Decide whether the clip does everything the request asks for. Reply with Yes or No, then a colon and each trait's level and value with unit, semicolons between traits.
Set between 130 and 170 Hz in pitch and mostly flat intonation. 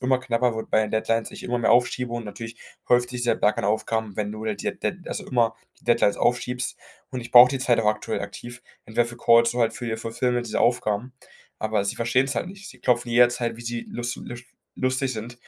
No: low, 120 Hz; narrow, 1.7 semitones